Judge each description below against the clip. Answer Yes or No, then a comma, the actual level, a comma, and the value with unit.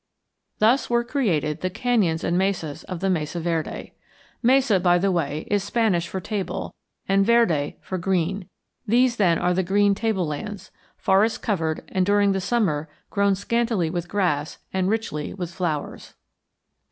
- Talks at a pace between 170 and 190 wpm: No, average, 155 wpm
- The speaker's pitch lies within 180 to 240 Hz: Yes, high, 190 Hz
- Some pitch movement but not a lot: Yes, average, 3.6 semitones